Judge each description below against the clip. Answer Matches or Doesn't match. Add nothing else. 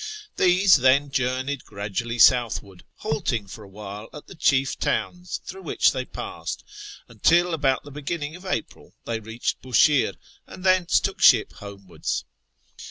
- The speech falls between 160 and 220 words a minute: Doesn't match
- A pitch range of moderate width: Doesn't match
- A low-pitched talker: Matches